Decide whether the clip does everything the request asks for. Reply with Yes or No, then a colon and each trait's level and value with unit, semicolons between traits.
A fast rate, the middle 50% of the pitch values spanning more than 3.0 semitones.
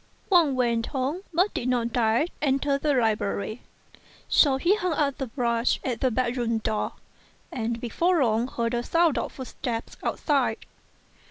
No: average, 155 wpm; average, 3.7 semitones